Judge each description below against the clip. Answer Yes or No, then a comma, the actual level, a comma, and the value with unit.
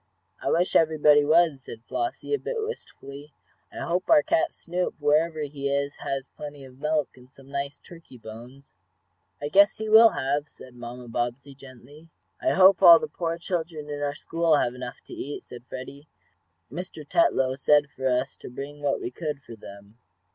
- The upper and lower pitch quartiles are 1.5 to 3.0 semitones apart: No, average, 3.9 semitones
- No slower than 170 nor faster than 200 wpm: Yes, average, 185 wpm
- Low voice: No, medium, 145 Hz